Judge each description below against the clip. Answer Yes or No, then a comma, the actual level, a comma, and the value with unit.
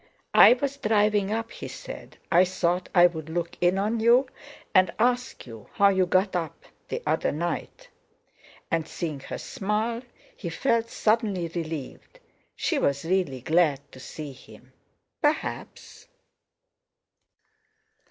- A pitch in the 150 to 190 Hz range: Yes, medium, 185 Hz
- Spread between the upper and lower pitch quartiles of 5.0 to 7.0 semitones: Yes, wide, 5.4 semitones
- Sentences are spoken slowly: Yes, slow, 125 wpm